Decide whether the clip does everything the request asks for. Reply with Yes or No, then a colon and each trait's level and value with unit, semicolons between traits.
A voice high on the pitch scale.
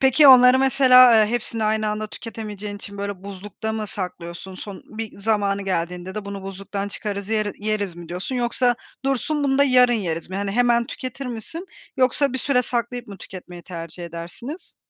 Yes: high, 215 Hz